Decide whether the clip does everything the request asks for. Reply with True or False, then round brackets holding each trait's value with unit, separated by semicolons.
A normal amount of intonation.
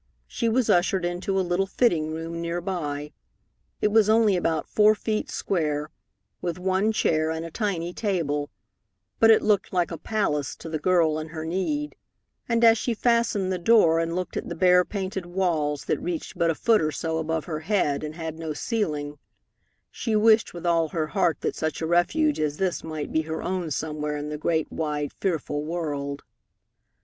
True (3.8 semitones)